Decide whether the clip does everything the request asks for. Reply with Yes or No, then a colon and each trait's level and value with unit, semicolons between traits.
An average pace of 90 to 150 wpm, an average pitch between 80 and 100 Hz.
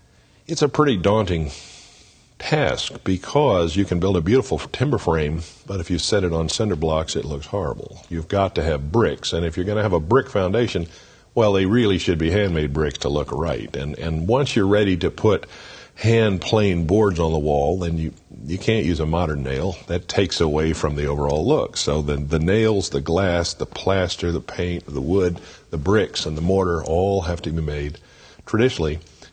No: fast, 205 wpm; very low, 85 Hz